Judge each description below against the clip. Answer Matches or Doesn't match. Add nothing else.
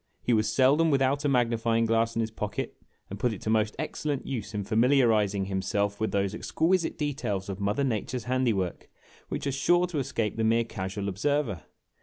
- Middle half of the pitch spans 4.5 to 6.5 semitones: Matches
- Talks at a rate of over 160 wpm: Matches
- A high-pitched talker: Doesn't match